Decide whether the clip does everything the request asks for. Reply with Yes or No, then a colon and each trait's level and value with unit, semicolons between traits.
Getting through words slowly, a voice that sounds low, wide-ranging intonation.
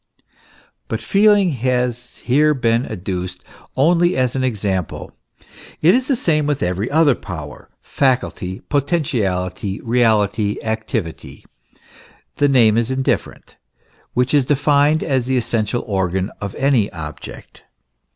Yes: slow, 120 wpm; low, 125 Hz; wide, 5.8 semitones